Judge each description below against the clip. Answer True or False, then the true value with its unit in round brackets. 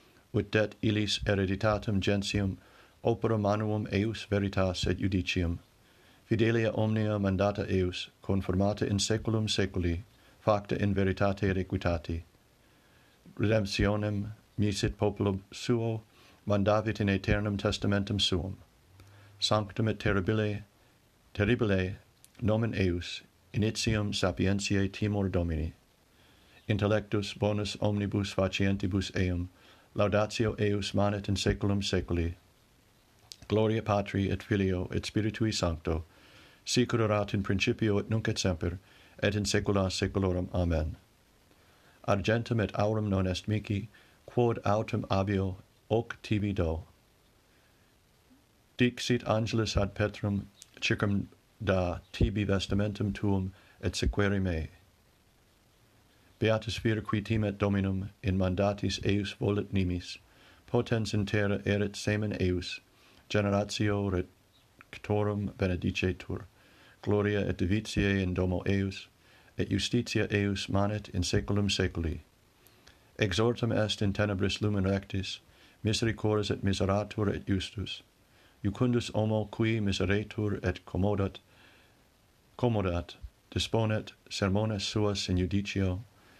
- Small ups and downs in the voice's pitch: True (2.0 semitones)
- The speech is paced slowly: True (105 wpm)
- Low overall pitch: True (100 Hz)